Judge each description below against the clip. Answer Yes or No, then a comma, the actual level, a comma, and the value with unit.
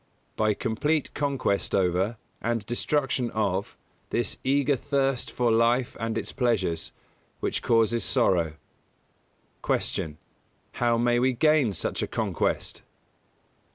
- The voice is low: Yes, low, 120 Hz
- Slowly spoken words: Yes, slow, 120 wpm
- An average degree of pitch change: Yes, average, 3.3 semitones